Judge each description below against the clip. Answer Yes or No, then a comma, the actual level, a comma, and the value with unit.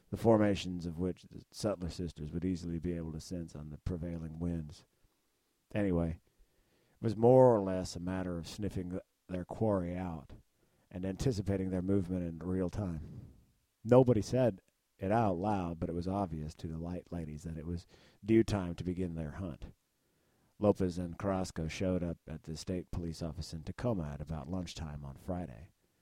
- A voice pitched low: Yes, very low, 90 Hz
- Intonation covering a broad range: No, average, 2.8 semitones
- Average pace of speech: Yes, average, 175 wpm